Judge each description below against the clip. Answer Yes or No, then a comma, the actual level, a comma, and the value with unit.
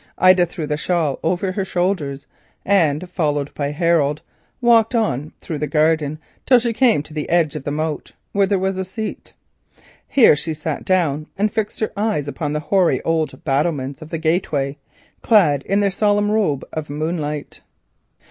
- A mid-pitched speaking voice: Yes, medium, 165 Hz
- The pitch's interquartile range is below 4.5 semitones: No, average, 4.8 semitones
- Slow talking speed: No, average, 175 wpm